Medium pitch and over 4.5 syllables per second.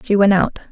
No: high, 195 Hz; 5.8 syllables/s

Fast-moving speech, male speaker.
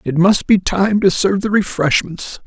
No: average, 195 wpm; male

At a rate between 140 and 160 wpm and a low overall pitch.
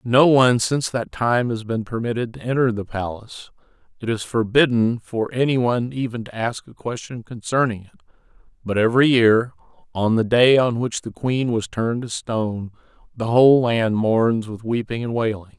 No: average, 175 wpm; low, 115 Hz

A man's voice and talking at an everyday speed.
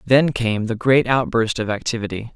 Yes: male; average, 180 wpm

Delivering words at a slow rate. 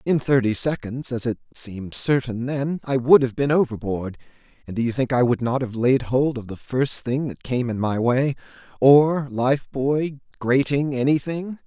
No: average, 180 wpm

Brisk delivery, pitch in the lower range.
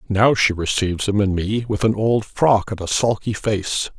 Yes: fast, 210 wpm; low, 105 Hz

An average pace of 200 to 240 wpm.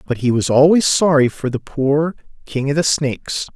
Yes: fast, 205 wpm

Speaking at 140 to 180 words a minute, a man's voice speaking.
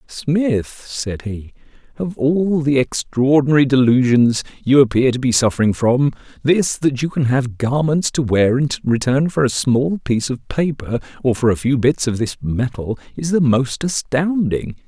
Yes: average, 170 wpm; male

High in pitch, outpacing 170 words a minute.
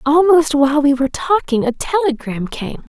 No: very high, 290 Hz; average, 165 wpm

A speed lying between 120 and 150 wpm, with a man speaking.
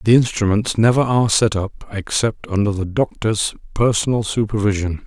Yes: average, 140 wpm; male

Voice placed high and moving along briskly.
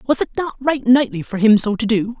Yes: high, 235 Hz; fast, 275 wpm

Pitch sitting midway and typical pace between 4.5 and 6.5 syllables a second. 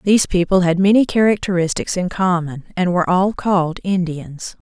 Yes: medium, 180 Hz; 5.3 syllables/s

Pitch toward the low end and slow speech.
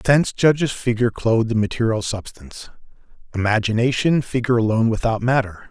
Yes: low, 115 Hz; slow, 125 wpm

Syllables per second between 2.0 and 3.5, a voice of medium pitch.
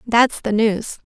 No: 3.3 syllables/s; high, 220 Hz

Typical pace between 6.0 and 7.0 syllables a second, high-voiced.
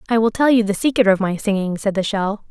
Yes: 6.2 syllables/s; high, 210 Hz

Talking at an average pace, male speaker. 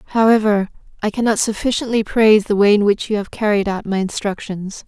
No: average, 185 wpm; female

